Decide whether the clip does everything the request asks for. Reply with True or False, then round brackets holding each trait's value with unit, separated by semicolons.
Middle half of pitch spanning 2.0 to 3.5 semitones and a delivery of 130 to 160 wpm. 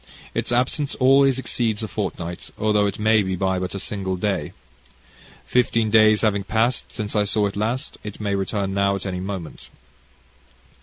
False (2.4 semitones; 170 wpm)